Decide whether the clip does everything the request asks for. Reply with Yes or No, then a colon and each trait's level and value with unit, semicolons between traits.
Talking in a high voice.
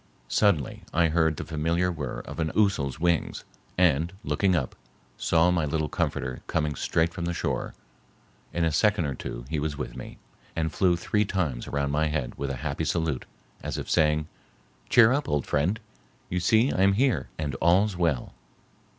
No: very low, 80 Hz